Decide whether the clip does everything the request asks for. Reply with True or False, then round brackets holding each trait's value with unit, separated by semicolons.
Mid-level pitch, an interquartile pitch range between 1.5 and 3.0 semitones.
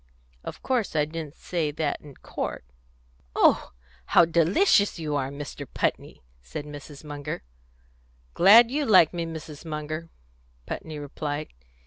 True (155 Hz; 2.6 semitones)